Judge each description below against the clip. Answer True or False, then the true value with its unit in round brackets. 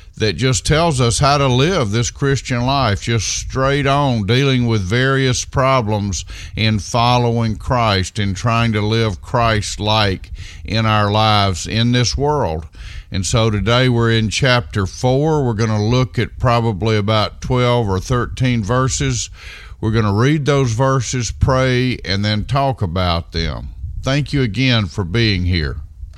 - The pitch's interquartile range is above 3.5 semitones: True (4.3 semitones)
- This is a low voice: True (115 Hz)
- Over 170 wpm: False (155 wpm)